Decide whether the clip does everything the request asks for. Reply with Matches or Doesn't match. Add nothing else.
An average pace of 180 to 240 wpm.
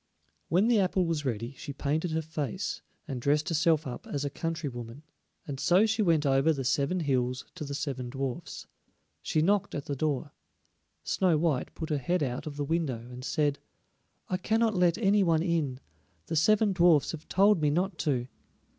Matches